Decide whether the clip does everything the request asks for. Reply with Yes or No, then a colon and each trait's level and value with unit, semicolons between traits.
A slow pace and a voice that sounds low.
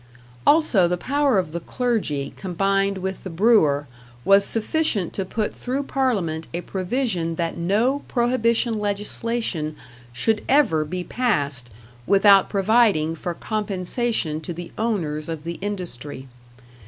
No: slow, 130 wpm; high, 195 Hz